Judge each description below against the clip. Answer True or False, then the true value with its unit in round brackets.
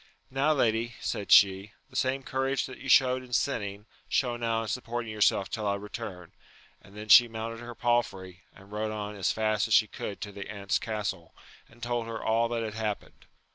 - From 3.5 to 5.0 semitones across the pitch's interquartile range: False (2.7 semitones)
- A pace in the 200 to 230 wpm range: True (205 wpm)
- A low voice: True (110 Hz)